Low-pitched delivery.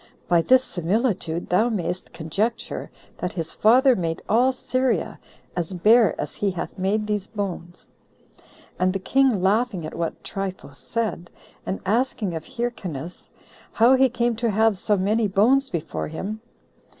No: high, 205 Hz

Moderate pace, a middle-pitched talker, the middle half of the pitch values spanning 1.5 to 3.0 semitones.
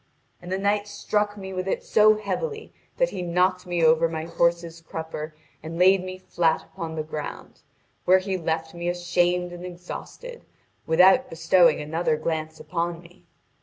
Yes: average, 165 wpm; medium, 175 Hz; narrow, 2.6 semitones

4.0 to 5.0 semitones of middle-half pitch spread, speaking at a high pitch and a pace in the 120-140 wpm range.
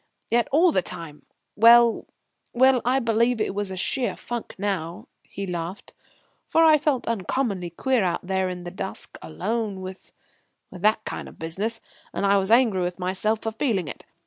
No: average, 4.3 semitones; high, 205 Hz; average, 175 wpm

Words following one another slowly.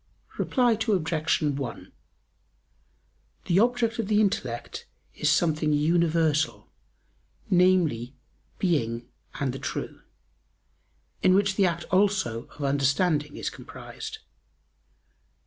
Yes: slow, 95 wpm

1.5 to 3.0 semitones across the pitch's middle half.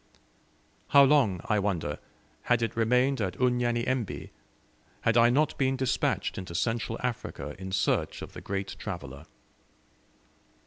No: average, 4.6 semitones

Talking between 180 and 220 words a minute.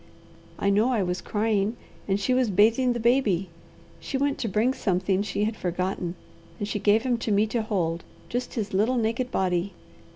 Yes: average, 190 wpm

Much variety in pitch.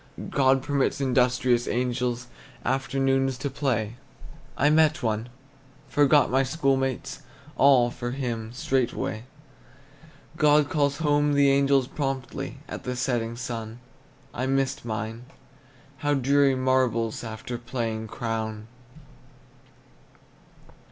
No: narrow, 2.6 semitones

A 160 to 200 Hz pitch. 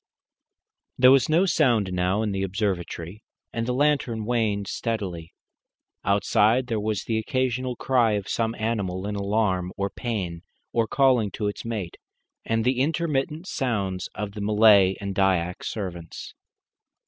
No: low, 110 Hz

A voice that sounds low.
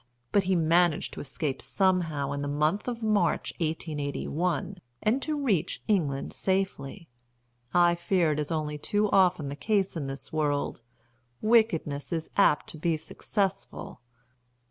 No: medium, 170 Hz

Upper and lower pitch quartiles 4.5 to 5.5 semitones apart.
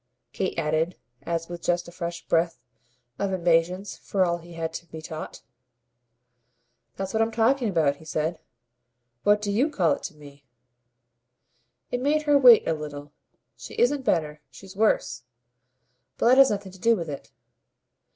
Yes: average, 4.8 semitones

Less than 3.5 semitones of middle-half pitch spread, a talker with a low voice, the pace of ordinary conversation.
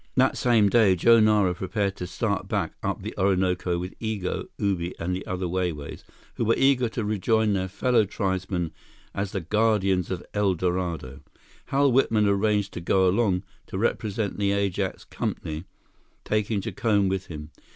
Yes: average, 2.9 semitones; low, 100 Hz; average, 165 wpm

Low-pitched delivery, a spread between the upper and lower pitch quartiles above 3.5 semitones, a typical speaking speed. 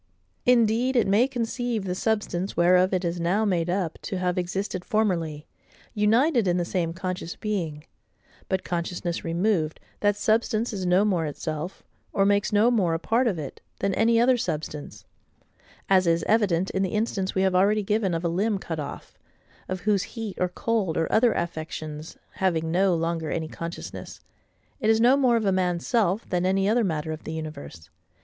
No: medium, 185 Hz; average, 4.2 semitones; average, 185 wpm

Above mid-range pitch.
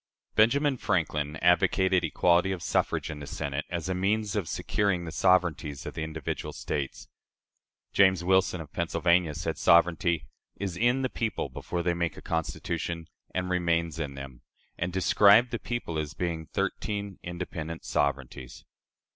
No: very low, 85 Hz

